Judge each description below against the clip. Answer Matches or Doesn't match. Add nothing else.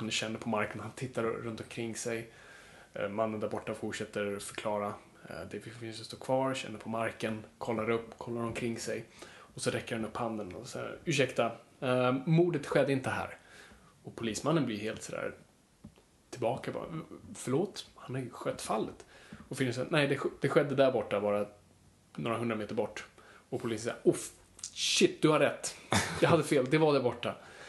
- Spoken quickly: Doesn't match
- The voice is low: Matches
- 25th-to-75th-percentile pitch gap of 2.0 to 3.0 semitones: Matches